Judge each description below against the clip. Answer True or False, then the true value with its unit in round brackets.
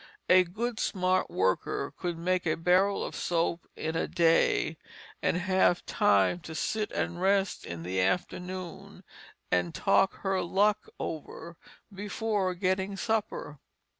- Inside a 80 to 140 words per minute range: True (135 wpm)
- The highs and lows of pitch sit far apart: False (2.8 semitones)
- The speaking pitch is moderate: True (180 Hz)